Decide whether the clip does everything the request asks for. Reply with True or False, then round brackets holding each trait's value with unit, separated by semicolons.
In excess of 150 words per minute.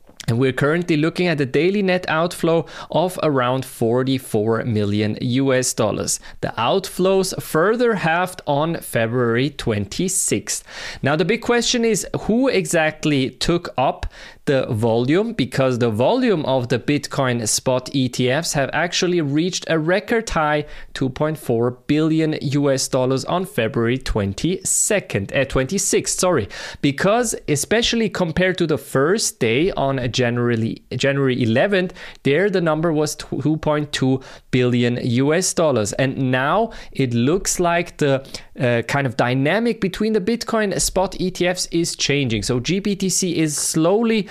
False (135 wpm)